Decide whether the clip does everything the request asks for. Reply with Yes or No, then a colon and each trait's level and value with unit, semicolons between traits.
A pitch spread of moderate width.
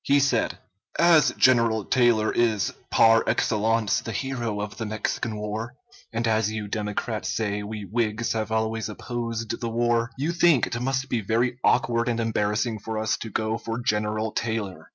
No: narrow, 1.6 semitones